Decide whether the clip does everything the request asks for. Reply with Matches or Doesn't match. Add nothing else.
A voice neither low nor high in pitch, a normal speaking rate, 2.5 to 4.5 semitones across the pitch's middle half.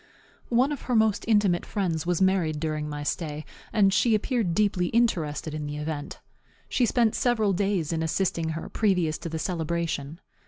Doesn't match